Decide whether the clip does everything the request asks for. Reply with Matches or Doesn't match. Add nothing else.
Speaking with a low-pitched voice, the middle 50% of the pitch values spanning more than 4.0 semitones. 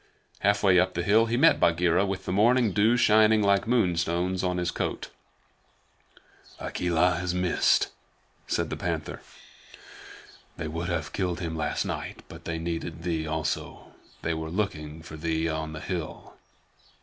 Doesn't match